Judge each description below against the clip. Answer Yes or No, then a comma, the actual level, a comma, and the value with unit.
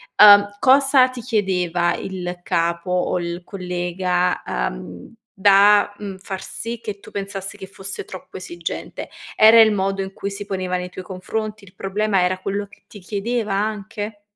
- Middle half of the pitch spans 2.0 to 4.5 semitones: Yes, narrow, 2.4 semitones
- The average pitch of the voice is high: Yes, high, 195 Hz